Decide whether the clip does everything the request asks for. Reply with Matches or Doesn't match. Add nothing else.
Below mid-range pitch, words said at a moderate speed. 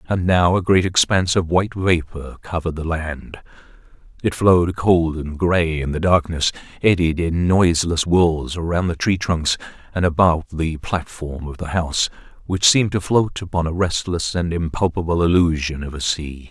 Matches